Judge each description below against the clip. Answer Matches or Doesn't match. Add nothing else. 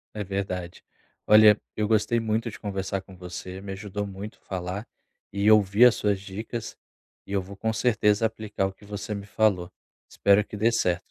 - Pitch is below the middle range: Matches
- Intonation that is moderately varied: Doesn't match